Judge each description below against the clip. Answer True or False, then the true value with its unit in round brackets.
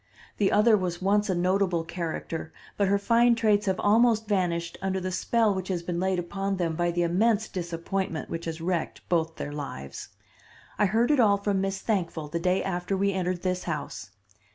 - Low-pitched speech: False (185 Hz)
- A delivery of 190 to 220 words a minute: True (195 wpm)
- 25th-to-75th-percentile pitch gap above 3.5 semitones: False (2.9 semitones)